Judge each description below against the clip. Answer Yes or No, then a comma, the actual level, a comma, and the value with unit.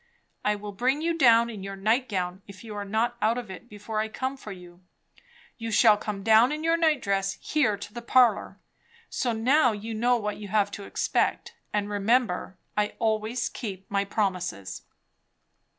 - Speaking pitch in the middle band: No, high, 215 Hz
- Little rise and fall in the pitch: No, average, 3.2 semitones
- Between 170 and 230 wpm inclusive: Yes, average, 180 wpm